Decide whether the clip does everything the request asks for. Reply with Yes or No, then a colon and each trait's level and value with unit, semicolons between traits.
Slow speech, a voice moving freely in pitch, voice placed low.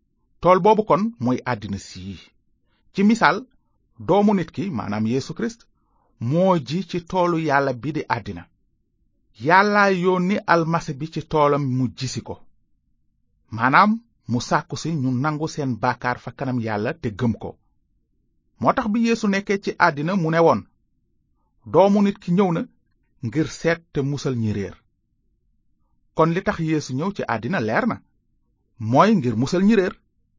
No: slow, 135 wpm; wide, 7.9 semitones; medium, 145 Hz